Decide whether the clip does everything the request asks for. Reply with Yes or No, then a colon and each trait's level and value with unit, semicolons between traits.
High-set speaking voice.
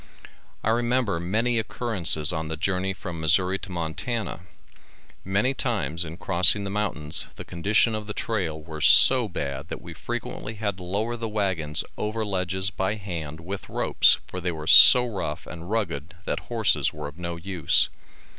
No: very low, 95 Hz